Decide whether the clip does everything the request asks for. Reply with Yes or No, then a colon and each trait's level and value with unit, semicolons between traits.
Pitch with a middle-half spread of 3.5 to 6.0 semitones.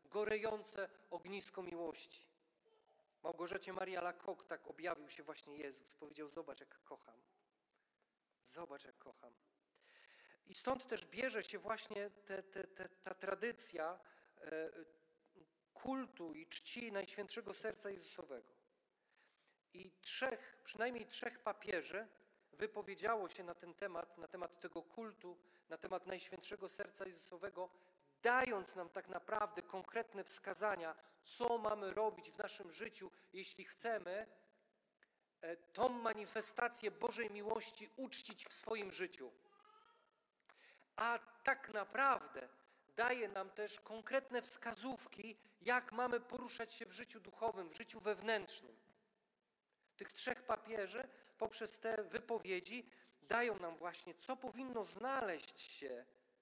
Yes: average, 4.2 semitones